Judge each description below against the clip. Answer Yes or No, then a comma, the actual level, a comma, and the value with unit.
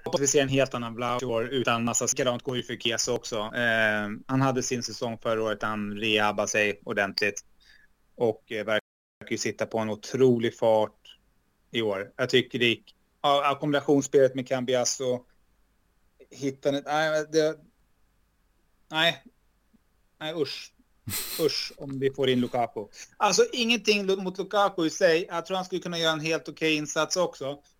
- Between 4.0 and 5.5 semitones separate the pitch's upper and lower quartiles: Yes, average, 5.2 semitones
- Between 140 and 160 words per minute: Yes, average, 155 wpm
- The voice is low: Yes, low, 130 Hz